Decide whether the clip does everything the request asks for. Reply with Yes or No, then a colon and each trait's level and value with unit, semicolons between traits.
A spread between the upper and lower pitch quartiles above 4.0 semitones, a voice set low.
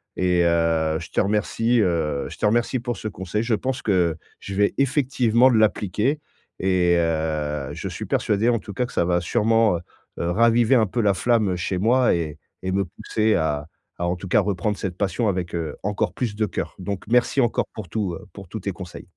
Yes: average, 4.6 semitones; low, 100 Hz